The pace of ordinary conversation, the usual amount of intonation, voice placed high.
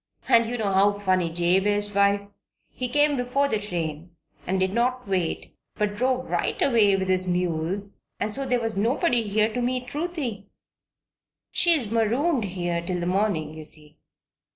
Yes: average, 170 wpm; average, 5.0 semitones; high, 205 Hz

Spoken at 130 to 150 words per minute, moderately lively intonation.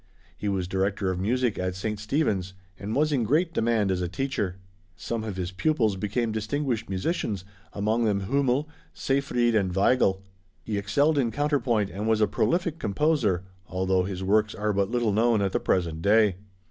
No: average, 175 wpm; average, 4.2 semitones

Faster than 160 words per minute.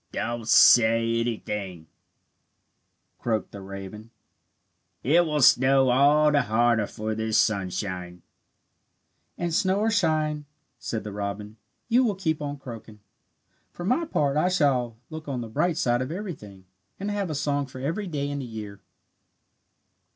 No: average, 145 wpm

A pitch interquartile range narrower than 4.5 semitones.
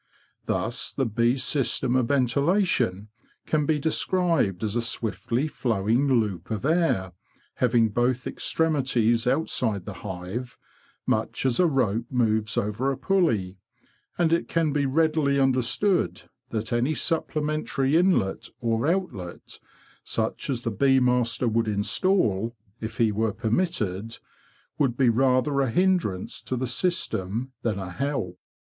No: average, 4.9 semitones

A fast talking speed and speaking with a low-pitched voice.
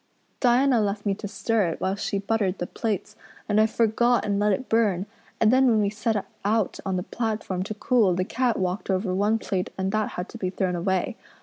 No: fast, 225 wpm; high, 205 Hz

